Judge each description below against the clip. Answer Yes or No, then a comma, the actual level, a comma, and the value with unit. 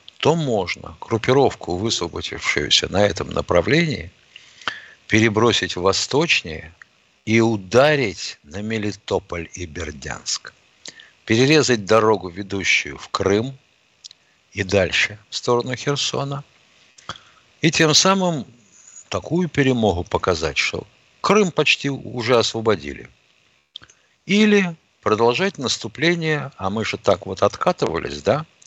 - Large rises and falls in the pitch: Yes, wide, 6.4 semitones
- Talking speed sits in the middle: No, slow, 100 wpm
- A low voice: Yes, low, 115 Hz